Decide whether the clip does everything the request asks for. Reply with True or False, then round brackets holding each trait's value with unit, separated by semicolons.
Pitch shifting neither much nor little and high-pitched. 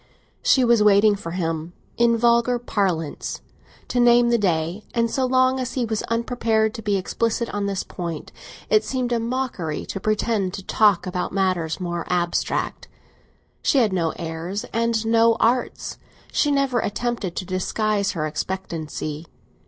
True (4.7 semitones; 215 Hz)